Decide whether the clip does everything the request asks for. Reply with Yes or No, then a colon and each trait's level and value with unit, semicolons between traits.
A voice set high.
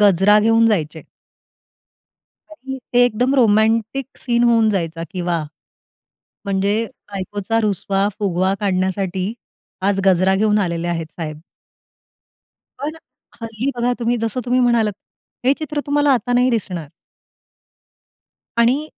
Yes: high, 210 Hz